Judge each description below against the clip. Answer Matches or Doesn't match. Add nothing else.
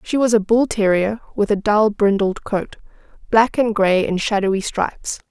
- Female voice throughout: Matches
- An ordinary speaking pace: Matches